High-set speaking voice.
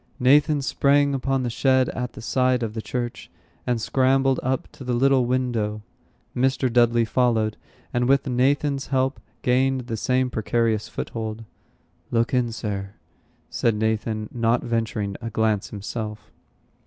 No: low, 120 Hz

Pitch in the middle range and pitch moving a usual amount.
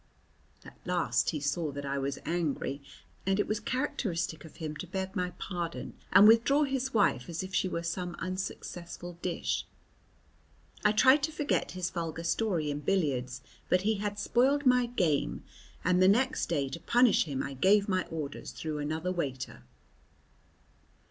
Yes: medium, 180 Hz; average, 4.9 semitones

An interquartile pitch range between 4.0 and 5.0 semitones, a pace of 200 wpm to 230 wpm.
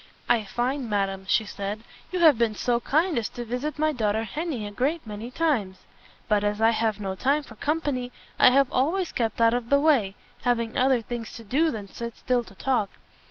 Yes: average, 4.5 semitones; fast, 205 wpm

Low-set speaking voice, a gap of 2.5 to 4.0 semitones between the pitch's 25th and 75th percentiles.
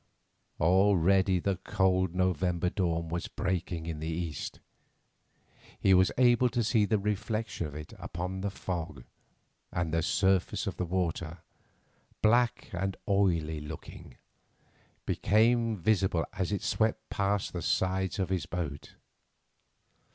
Yes: very low, 95 Hz; average, 3.1 semitones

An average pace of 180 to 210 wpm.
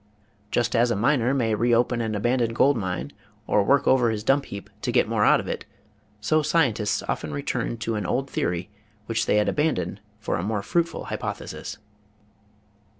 Yes: average, 185 wpm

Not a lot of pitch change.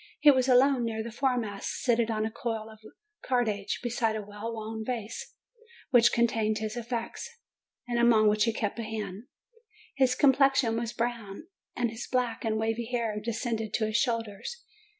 Yes: narrow, 1.9 semitones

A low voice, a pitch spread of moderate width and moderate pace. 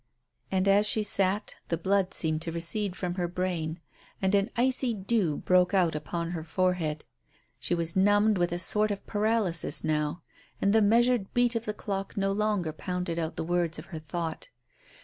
No: medium, 185 Hz; average, 3.5 semitones; average, 185 wpm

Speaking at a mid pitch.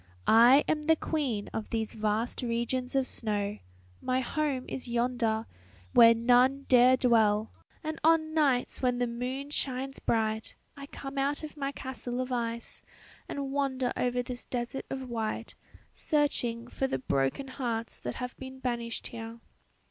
No: very high, 250 Hz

